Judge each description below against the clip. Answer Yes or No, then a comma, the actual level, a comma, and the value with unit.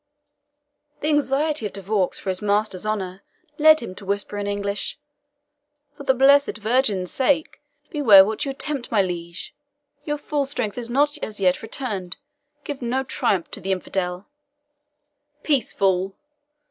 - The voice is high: Yes, high, 215 Hz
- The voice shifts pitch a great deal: Yes, wide, 5.9 semitones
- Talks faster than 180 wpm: No, average, 150 wpm